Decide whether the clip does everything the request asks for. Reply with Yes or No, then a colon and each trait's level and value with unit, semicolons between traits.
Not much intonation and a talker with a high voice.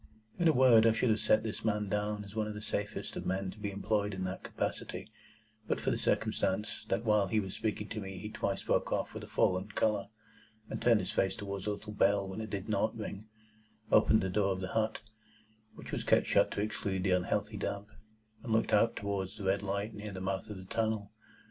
No: narrow, 2.0 semitones; low, 105 Hz